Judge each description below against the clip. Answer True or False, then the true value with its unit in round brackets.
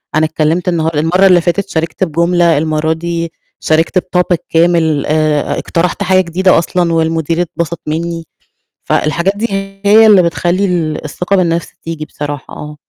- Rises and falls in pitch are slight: True (2.1 semitones)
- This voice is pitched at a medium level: True (170 Hz)